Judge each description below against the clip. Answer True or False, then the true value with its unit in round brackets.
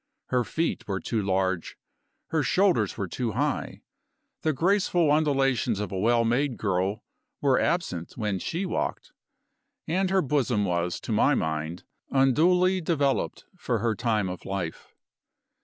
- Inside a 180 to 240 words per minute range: False (140 wpm)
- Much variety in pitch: True (8.3 semitones)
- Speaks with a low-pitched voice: True (120 Hz)